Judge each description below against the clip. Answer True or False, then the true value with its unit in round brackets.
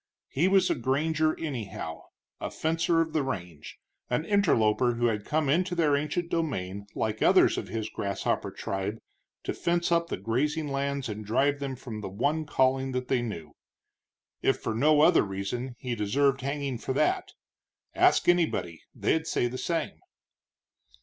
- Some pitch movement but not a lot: False (6.2 semitones)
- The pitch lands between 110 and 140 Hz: True (135 Hz)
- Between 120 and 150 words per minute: False (165 wpm)